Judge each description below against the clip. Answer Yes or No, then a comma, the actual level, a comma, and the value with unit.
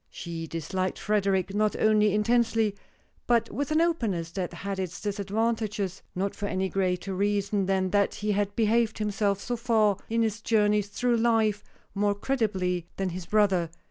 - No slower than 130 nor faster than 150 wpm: No, average, 160 wpm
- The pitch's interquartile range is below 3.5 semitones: Yes, narrow, 2.5 semitones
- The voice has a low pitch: No, high, 205 Hz